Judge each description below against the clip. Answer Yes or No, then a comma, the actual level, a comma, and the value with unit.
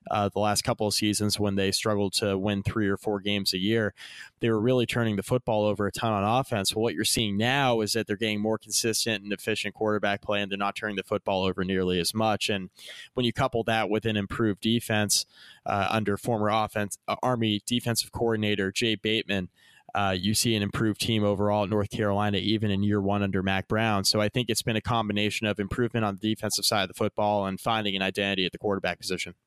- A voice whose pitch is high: No, low, 105 Hz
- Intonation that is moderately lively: No, narrow, 1.8 semitones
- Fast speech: Yes, fast, 230 wpm